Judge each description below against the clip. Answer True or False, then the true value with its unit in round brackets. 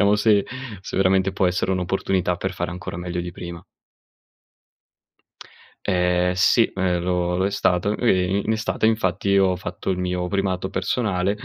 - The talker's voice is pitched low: True (95 Hz)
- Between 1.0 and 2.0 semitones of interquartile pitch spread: True (1.7 semitones)